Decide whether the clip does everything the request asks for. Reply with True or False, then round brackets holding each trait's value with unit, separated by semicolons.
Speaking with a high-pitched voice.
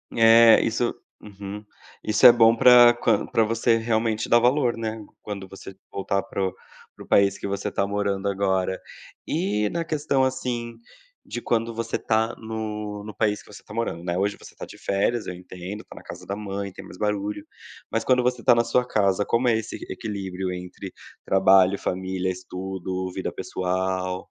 False (105 Hz)